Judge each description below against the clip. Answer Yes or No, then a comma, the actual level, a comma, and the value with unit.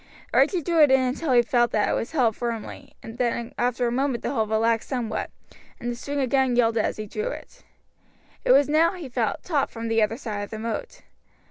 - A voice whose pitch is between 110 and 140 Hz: No, high, 240 Hz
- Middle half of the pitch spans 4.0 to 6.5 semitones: No, average, 3.5 semitones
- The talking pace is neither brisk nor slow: No, fast, 220 wpm